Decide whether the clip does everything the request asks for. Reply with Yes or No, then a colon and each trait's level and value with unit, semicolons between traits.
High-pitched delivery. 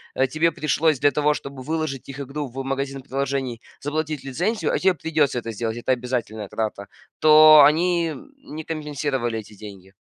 No: medium, 140 Hz